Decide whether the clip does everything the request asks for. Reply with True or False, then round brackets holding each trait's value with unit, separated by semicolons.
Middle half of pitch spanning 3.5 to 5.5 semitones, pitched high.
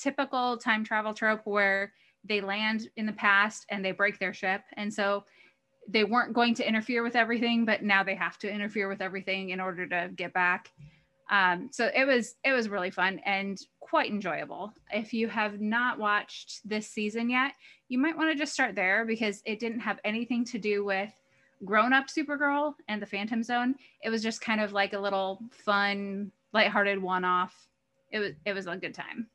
False (3.1 semitones; 215 Hz)